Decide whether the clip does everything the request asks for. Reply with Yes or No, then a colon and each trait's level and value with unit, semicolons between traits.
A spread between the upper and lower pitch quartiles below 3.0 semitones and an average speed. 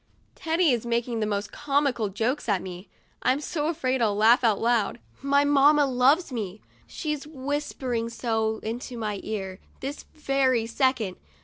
No: average, 4.4 semitones; average, 150 wpm